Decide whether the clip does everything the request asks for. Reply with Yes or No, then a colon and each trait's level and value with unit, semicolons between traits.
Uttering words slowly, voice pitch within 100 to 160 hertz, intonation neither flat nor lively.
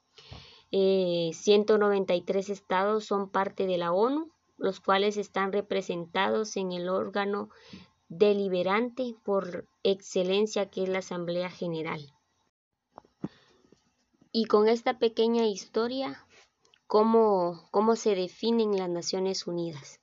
No: slow, 110 wpm; high, 200 Hz; average, 3.0 semitones